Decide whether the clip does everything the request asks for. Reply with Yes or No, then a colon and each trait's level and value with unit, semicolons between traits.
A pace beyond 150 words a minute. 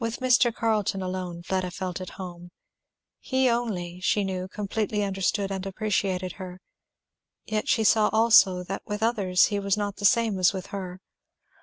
Yes: average, 165 wpm